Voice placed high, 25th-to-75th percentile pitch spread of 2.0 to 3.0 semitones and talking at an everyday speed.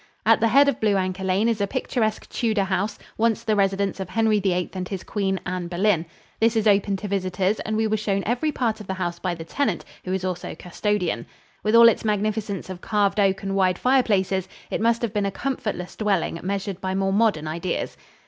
No: high, 200 Hz; narrow, 2.6 semitones; fast, 215 wpm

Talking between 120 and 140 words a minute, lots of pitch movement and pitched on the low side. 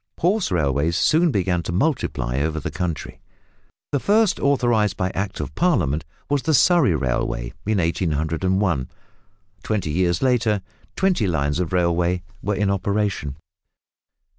Yes: slow, 135 wpm; wide, 7.0 semitones; very low, 95 Hz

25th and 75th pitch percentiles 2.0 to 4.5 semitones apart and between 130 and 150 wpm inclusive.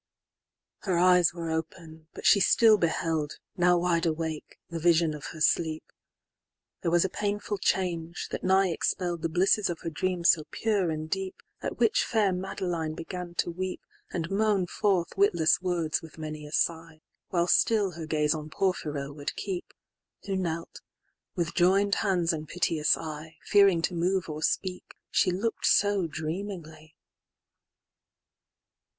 Yes: average, 2.8 semitones; slow, 135 wpm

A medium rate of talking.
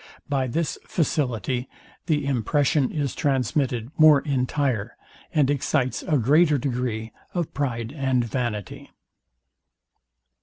No: slow, 105 wpm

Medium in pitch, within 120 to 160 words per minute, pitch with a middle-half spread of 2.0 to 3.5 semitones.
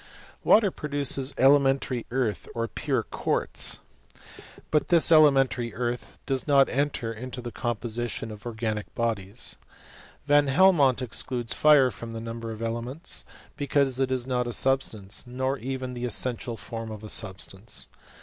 No: low, 125 Hz; average, 145 wpm; average, 2.9 semitones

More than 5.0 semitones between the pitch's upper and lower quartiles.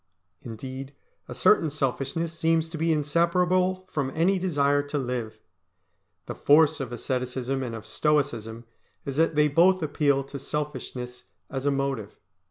No: average, 3.9 semitones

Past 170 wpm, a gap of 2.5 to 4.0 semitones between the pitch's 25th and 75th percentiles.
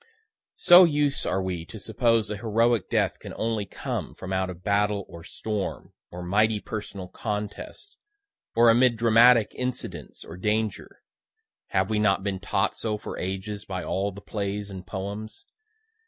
No: average, 155 wpm; average, 2.9 semitones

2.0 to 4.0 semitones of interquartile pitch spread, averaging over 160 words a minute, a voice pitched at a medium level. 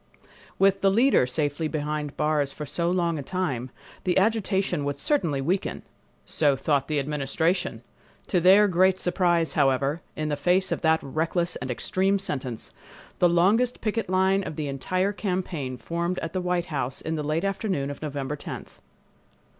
No: average, 4.4 semitones; average, 170 wpm; medium, 170 Hz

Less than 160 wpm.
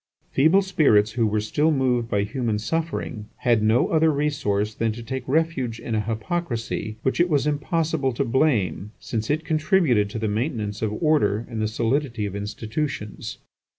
No: average, 170 wpm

